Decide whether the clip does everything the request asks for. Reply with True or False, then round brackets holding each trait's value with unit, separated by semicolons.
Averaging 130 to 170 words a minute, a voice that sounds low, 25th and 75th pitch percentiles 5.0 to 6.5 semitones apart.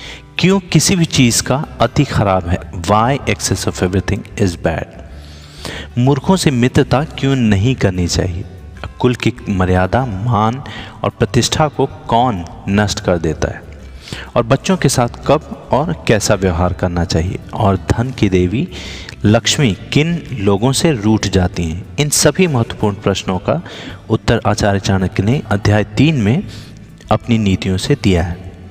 True (150 wpm; 105 Hz; 5.3 semitones)